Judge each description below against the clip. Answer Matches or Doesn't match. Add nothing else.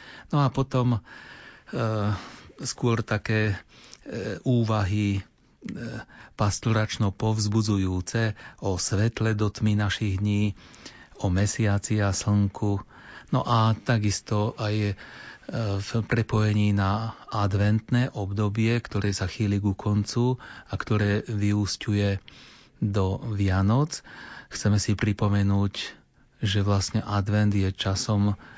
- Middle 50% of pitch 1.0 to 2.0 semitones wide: Matches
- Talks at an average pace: Doesn't match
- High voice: Doesn't match